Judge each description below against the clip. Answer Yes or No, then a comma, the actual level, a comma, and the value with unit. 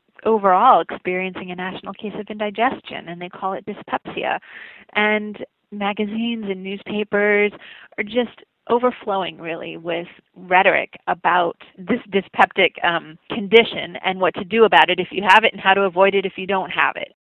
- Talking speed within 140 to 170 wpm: Yes, average, 165 wpm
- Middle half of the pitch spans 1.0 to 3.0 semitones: Yes, narrow, 2.5 semitones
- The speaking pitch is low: No, high, 195 Hz